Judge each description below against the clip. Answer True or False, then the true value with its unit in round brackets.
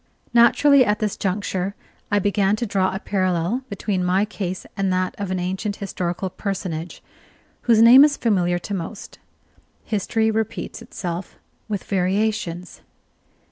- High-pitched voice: True (195 Hz)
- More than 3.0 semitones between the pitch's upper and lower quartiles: False (2.7 semitones)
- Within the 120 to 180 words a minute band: True (140 wpm)